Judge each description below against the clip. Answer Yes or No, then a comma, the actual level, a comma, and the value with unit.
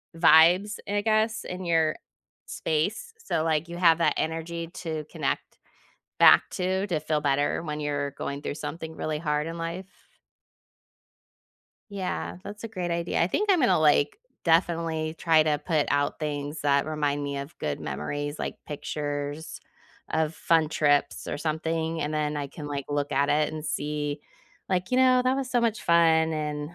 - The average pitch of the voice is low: No, medium, 160 Hz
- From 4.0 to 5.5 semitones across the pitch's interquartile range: No, narrow, 2.6 semitones